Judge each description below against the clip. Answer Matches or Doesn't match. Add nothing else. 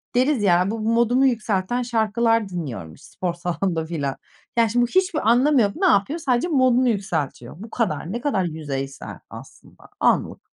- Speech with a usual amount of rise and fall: Doesn't match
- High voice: Matches